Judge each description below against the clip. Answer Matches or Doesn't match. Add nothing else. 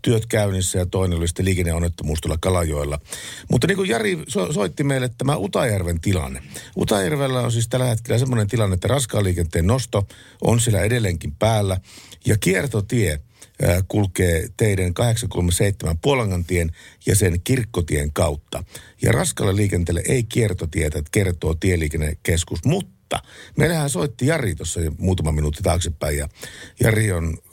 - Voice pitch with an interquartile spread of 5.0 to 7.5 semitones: Matches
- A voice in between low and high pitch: Doesn't match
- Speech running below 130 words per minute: Doesn't match